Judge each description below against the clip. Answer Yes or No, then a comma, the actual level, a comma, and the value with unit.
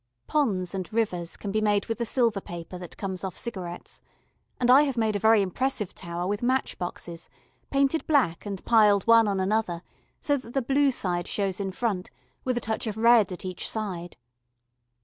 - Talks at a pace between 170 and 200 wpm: Yes, average, 190 wpm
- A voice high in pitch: Yes, high, 210 Hz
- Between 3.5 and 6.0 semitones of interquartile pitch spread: Yes, average, 4.3 semitones